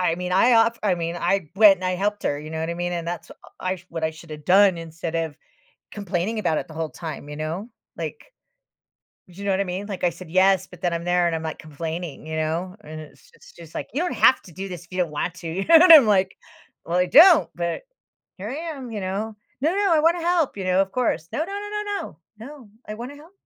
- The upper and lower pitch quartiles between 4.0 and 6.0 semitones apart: Yes, average, 4.6 semitones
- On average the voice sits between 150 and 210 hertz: Yes, medium, 185 Hz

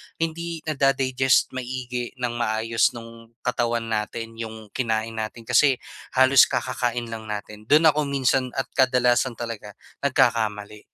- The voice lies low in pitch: Yes, low, 120 Hz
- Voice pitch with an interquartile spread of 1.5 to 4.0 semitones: Yes, average, 2.7 semitones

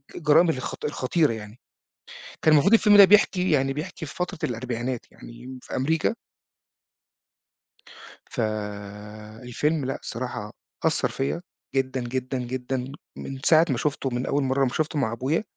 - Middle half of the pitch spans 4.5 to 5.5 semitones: No, average, 3.9 semitones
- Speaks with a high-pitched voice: No, low, 135 Hz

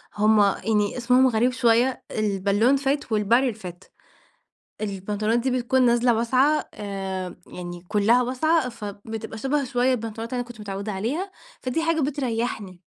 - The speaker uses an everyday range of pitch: Yes, average, 3.7 semitones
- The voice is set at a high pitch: Yes, high, 230 Hz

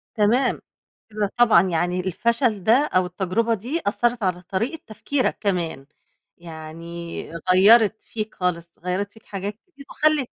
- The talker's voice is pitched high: Yes, high, 205 Hz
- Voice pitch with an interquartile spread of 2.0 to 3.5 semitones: No, average, 4.5 semitones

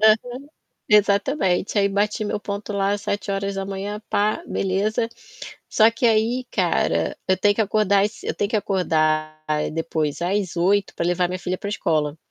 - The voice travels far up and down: No, average, 2.7 semitones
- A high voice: Yes, high, 200 Hz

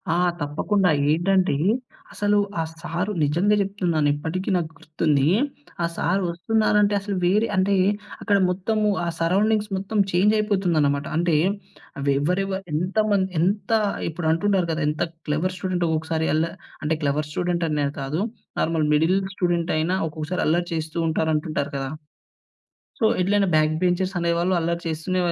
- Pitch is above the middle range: No, medium, 175 Hz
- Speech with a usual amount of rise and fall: Yes, average, 3.6 semitones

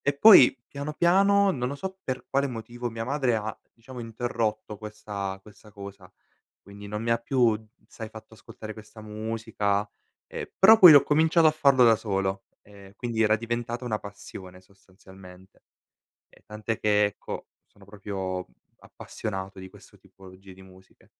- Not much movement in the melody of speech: No, average, 3.7 semitones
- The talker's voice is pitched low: Yes, low, 110 Hz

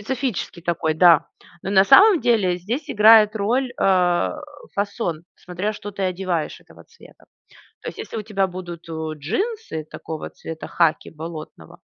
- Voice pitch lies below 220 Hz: Yes, medium, 185 Hz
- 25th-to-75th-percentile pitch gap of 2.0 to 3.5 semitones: No, average, 4.2 semitones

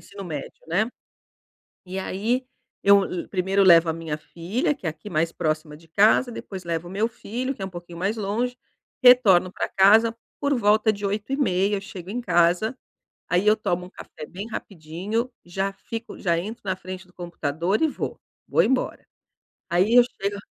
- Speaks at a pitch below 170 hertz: No, high, 195 Hz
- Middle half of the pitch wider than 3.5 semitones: Yes, average, 4.1 semitones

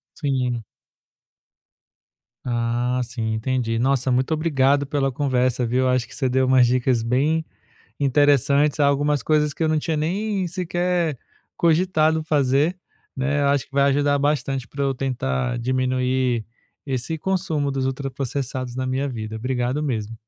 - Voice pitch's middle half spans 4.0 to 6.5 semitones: No, average, 2.9 semitones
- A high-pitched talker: No, low, 135 Hz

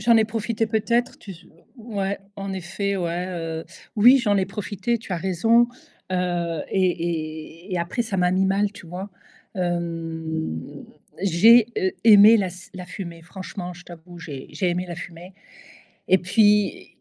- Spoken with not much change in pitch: No, average, 3.2 semitones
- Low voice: No, medium, 185 Hz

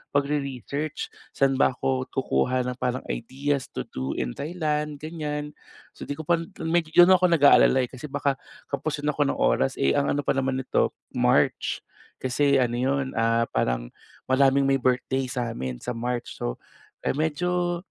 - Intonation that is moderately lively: Yes, average, 3.1 semitones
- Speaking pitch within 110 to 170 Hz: Yes, low, 135 Hz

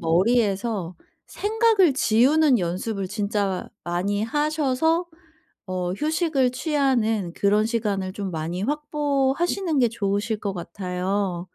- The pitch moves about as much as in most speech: No, wide, 7.3 semitones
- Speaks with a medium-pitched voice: No, high, 220 Hz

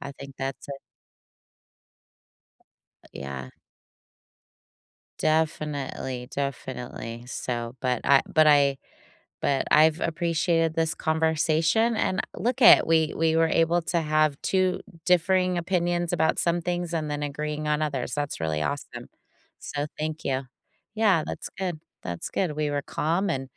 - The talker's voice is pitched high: No, medium, 155 Hz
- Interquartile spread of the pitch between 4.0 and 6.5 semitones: No, average, 3.4 semitones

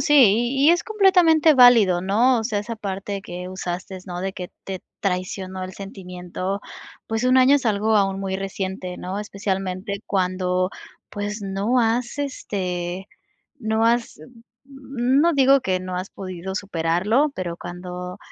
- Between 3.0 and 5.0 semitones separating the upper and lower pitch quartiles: Yes, average, 4.5 semitones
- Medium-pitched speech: No, high, 195 Hz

